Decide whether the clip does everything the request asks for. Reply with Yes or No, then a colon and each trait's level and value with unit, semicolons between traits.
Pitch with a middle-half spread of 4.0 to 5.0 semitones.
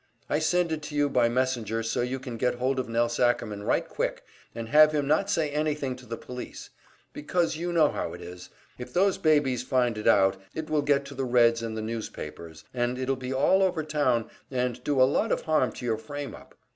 Yes: average, 4.3 semitones